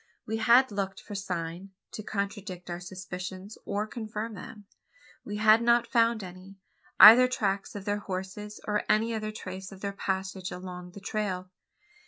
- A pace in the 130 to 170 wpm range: Yes, average, 160 wpm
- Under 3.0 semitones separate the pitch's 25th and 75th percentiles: Yes, narrow, 2.5 semitones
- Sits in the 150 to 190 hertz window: No, high, 200 Hz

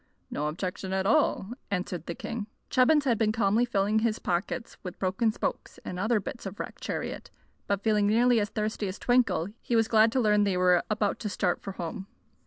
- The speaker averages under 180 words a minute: No, fast, 205 wpm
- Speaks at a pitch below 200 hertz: No, high, 210 Hz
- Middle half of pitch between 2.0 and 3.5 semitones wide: Yes, average, 3.2 semitones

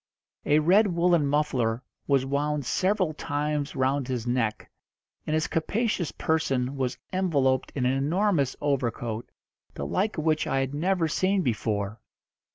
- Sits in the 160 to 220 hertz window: No, medium, 145 Hz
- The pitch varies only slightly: No, average, 4.4 semitones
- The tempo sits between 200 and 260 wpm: No, average, 145 wpm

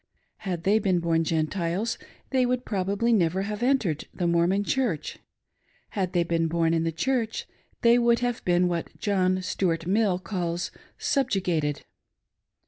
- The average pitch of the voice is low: No, medium, 185 Hz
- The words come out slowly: No, average, 155 wpm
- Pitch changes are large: No, average, 4.6 semitones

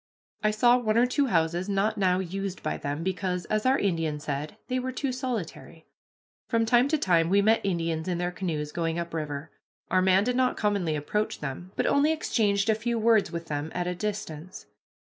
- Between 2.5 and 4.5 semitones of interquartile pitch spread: No, average, 5.2 semitones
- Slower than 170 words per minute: No, fast, 205 wpm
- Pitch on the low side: No, high, 190 Hz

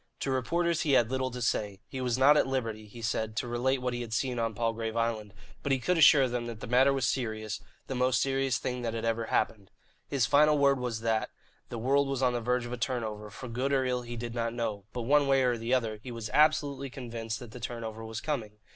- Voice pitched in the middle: No, low, 120 Hz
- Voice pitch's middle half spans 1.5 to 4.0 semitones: Yes, average, 2.7 semitones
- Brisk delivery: Yes, fast, 250 wpm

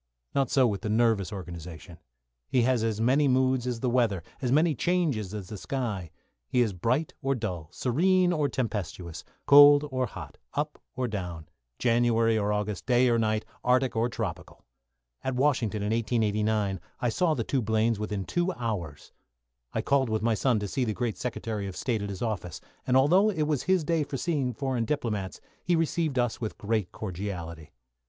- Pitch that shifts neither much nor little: Yes, average, 4.2 semitones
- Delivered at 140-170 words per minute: No, average, 185 wpm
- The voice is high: No, low, 115 Hz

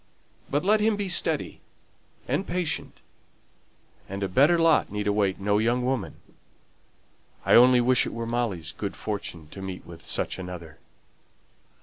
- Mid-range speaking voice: No, low, 110 Hz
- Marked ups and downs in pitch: Yes, wide, 6.0 semitones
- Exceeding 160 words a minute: No, average, 145 wpm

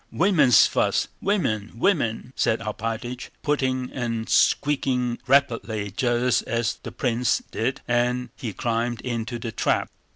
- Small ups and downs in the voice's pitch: Yes, narrow, 2.2 semitones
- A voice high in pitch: No, low, 120 Hz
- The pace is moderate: No, slow, 125 wpm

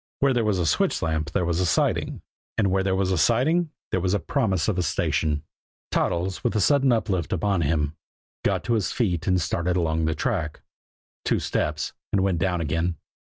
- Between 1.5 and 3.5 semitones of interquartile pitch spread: No, average, 4.2 semitones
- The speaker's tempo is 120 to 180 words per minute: No, average, 200 wpm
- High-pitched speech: No, very low, 90 Hz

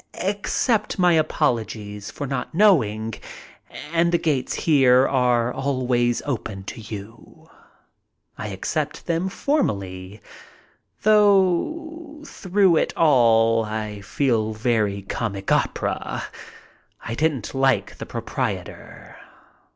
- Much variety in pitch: Yes, wide, 7.6 semitones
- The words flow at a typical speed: No, slow, 100 wpm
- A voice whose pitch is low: Yes, low, 130 Hz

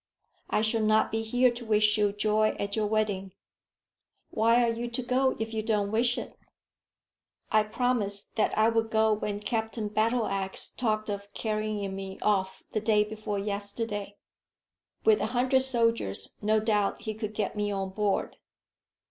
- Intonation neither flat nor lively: No, narrow, 1.7 semitones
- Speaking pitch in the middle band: No, high, 215 Hz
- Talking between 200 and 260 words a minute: No, average, 165 wpm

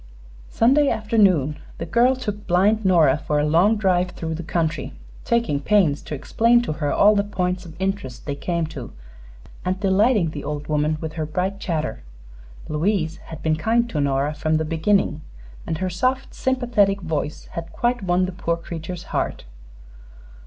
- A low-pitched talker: No, medium, 175 Hz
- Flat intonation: No, average, 4.9 semitones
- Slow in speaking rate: No, average, 170 wpm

